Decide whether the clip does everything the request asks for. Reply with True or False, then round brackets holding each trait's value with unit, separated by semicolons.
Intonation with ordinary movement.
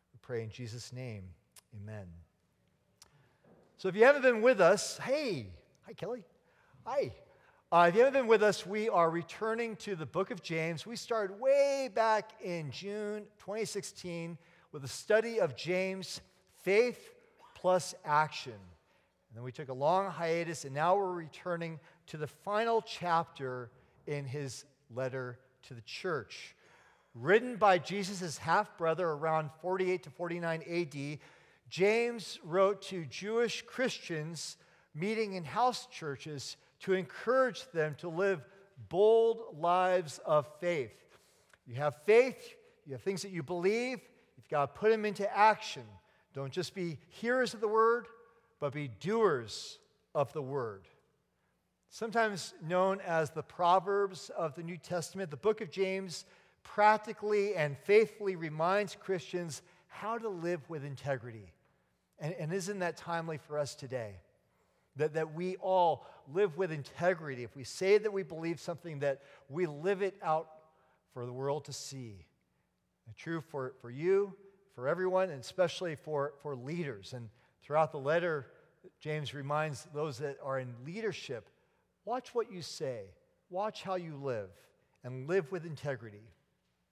False (5.9 semitones)